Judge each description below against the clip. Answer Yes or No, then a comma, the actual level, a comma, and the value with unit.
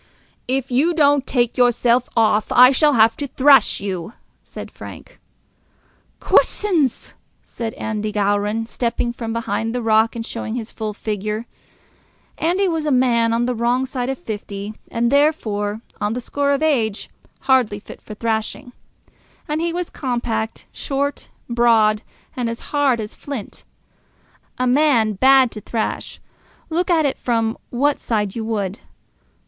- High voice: Yes, high, 235 Hz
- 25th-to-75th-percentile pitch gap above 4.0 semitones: No, average, 3.7 semitones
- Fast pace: No, average, 150 wpm